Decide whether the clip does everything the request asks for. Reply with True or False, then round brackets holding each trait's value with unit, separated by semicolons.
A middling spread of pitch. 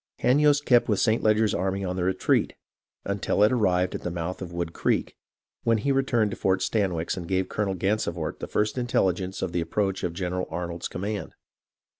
True (3.3 semitones)